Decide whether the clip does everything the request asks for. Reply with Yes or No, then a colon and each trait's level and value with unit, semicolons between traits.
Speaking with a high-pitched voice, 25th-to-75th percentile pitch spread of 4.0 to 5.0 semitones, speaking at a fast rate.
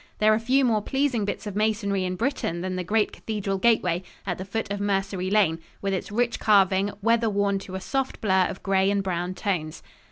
No: high, 200 Hz; narrow, 2.5 semitones; fast, 215 wpm